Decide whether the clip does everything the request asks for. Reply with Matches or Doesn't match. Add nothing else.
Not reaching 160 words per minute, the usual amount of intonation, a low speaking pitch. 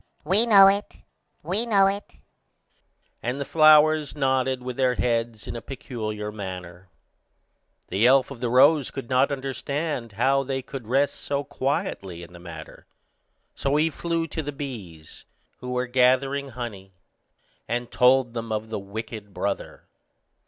Matches